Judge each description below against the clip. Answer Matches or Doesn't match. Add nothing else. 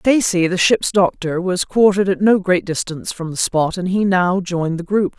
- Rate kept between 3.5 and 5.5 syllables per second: Matches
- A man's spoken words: Doesn't match